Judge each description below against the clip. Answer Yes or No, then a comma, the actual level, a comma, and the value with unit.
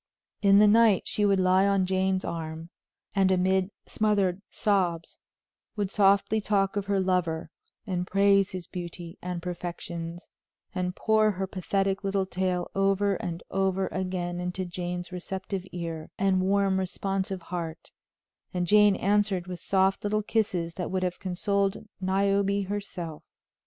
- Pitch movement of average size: No, narrow, 1.8 semitones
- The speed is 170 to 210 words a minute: No, average, 140 wpm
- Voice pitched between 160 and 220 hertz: Yes, high, 190 Hz